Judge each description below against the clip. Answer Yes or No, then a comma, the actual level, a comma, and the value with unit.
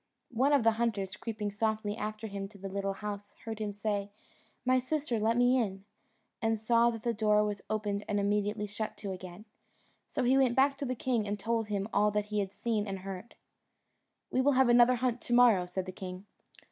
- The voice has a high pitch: Yes, high, 215 Hz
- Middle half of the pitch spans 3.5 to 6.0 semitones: No, average, 2.8 semitones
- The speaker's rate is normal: No, fast, 210 wpm